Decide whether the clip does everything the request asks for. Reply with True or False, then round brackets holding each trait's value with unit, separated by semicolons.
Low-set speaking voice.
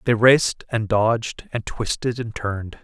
True (110 Hz)